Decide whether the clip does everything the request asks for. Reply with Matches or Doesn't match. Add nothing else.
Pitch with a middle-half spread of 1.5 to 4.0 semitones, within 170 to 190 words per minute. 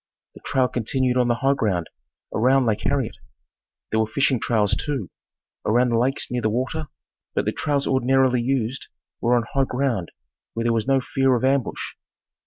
Matches